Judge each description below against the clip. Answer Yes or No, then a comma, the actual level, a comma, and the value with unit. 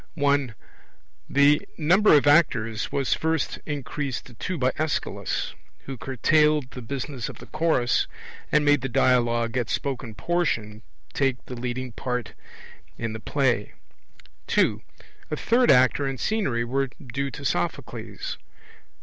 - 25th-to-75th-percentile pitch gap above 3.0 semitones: Yes, average, 3.4 semitones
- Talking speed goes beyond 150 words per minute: No, slow, 135 wpm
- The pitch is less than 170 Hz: Yes, low, 135 Hz